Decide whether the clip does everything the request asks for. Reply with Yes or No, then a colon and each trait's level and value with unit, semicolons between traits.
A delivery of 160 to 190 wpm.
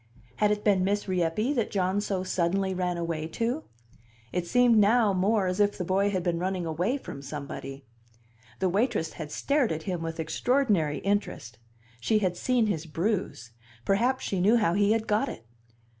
Yes: average, 180 wpm